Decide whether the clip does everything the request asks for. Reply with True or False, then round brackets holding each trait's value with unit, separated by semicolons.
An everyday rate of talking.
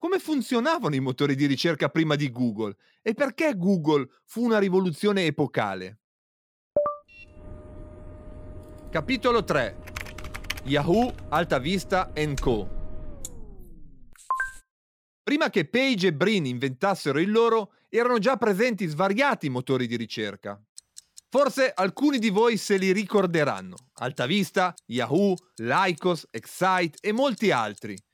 False (110 wpm)